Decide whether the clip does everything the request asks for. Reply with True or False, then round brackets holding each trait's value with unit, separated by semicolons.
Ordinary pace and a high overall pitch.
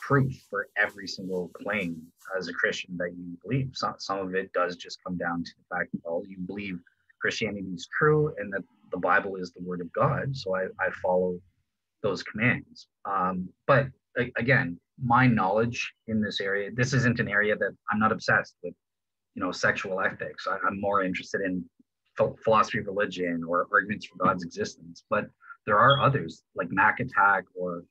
False (190 wpm; 95 Hz)